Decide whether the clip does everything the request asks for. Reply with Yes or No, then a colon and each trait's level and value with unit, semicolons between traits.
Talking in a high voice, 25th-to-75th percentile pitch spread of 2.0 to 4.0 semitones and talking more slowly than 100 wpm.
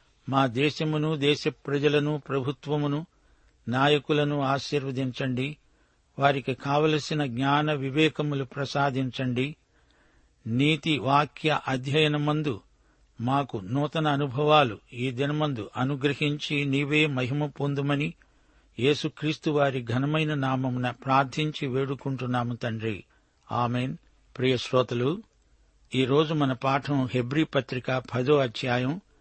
No: medium, 140 Hz; narrow, 2.5 semitones; average, 85 wpm